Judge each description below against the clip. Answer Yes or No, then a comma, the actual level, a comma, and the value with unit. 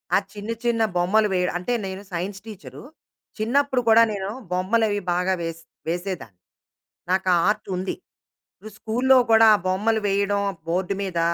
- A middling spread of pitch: Yes, average, 3.4 semitones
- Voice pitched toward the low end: No, high, 200 Hz